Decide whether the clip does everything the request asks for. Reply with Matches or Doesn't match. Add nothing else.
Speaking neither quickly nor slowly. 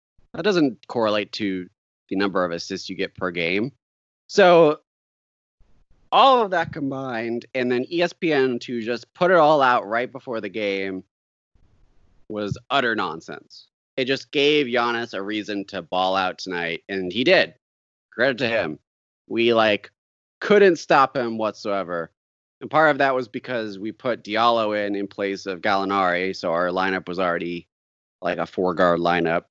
Matches